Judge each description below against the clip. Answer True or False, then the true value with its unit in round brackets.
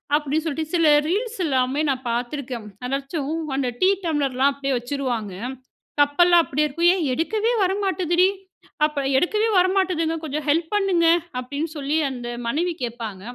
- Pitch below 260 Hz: False (300 Hz)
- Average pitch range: True (4.5 semitones)